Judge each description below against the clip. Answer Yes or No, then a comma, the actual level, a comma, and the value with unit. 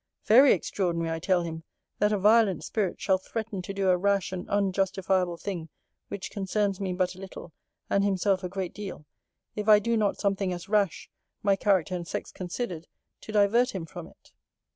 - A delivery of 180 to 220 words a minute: Yes, average, 185 wpm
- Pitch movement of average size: No, narrow, 2.2 semitones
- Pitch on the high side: Yes, high, 195 Hz